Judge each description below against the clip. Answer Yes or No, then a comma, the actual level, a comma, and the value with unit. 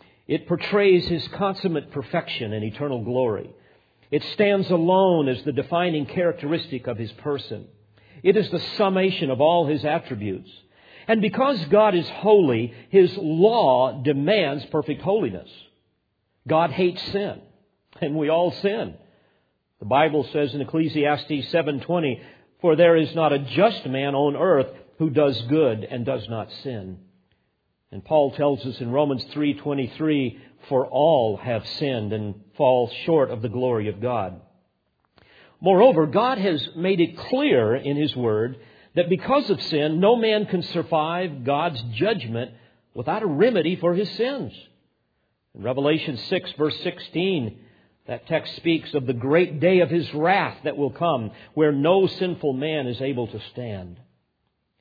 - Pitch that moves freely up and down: Yes, wide, 5.8 semitones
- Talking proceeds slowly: No, average, 150 wpm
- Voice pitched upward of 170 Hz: No, medium, 150 Hz